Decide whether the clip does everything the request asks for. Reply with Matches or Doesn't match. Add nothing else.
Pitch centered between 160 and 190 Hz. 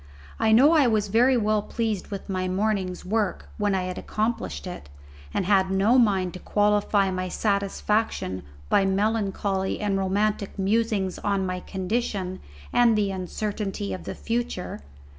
Doesn't match